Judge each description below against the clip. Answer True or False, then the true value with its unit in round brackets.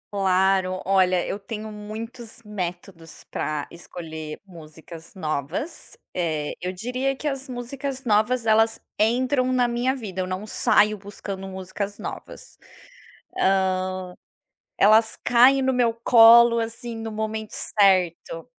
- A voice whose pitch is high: True (210 Hz)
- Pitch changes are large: False (4.3 semitones)